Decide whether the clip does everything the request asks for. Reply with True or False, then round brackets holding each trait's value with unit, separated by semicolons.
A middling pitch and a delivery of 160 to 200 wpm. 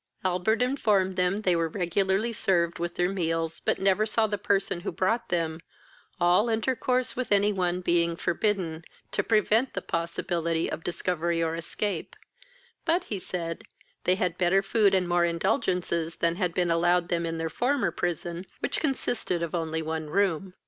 True (180 Hz; 170 wpm)